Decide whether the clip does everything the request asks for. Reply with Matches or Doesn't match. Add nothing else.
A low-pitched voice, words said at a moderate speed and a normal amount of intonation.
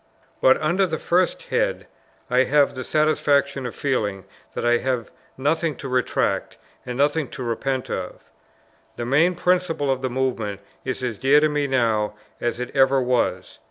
Matches